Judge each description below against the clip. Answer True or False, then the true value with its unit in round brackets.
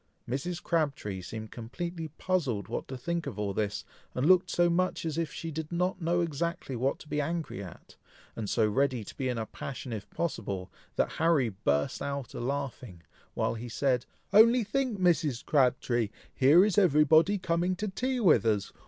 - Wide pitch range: True (6.7 semitones)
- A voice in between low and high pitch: True (145 Hz)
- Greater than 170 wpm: True (190 wpm)